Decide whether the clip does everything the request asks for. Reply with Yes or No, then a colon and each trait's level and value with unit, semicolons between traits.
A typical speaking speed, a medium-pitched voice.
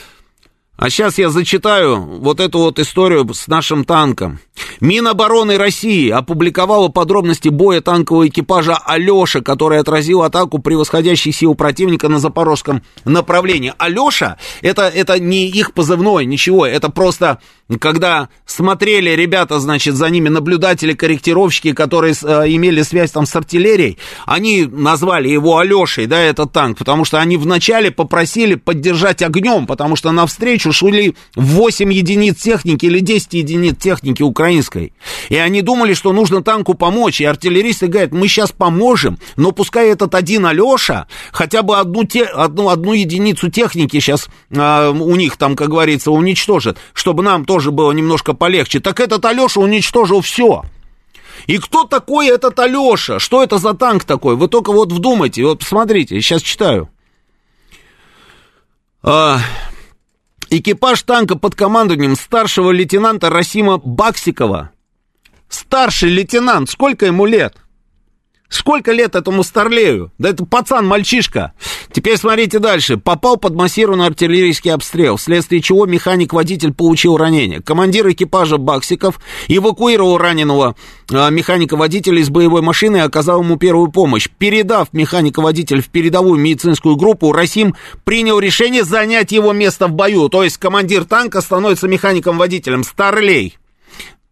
Yes: average, 135 wpm; medium, 180 Hz